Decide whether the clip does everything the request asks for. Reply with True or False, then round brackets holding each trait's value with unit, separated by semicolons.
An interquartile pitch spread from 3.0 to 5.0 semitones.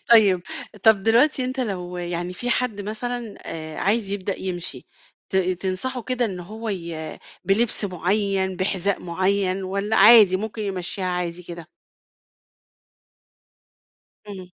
True (3.4 semitones)